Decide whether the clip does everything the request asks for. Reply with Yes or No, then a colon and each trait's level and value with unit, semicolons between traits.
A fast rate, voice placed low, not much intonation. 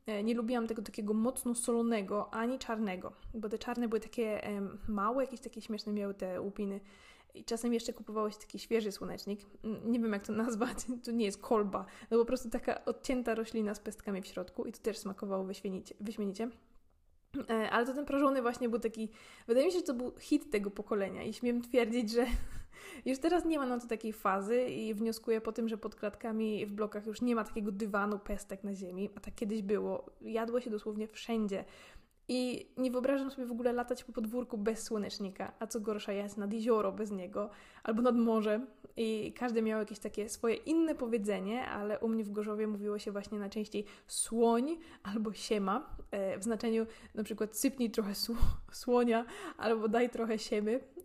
No: fast, 190 wpm; high, 225 Hz; narrow, 2.3 semitones